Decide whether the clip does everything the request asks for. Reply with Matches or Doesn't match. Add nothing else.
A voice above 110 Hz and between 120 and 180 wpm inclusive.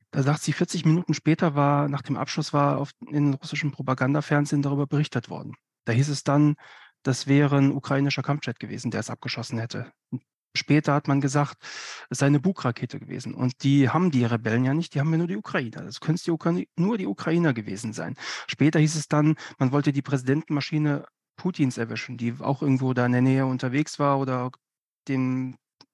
Doesn't match